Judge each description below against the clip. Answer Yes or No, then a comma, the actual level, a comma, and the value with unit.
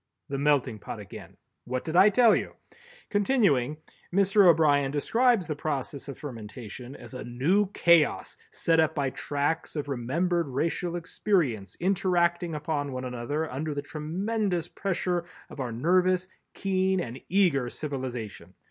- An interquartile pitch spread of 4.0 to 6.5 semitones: Yes, average, 5.3 semitones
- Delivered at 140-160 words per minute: Yes, average, 145 wpm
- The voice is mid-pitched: Yes, medium, 155 Hz